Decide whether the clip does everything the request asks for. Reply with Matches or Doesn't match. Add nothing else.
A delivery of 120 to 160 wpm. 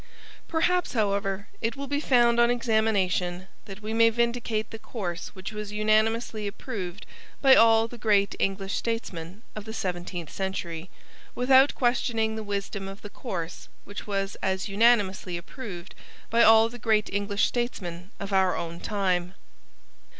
Matches